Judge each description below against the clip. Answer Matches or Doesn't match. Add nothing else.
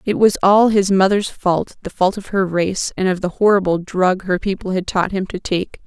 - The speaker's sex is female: Matches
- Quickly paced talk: Matches